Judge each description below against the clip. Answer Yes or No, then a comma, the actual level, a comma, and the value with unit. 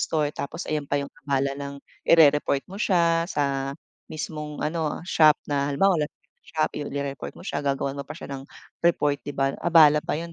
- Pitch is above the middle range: No, medium, 150 Hz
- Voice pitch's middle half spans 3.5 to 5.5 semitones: No, narrow, 2.4 semitones